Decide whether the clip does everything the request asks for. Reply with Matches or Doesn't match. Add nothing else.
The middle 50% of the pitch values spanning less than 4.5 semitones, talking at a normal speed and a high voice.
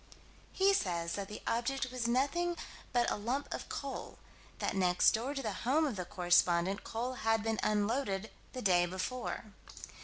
Doesn't match